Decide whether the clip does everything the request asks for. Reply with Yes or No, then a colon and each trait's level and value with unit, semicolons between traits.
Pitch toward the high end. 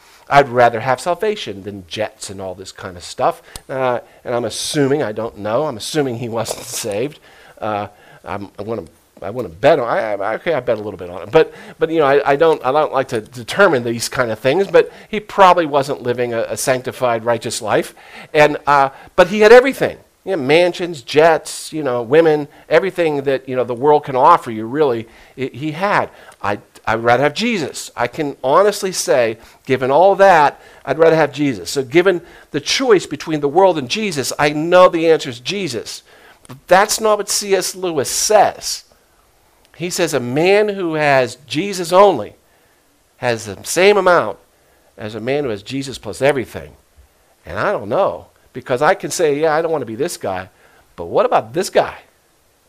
No: medium, 145 Hz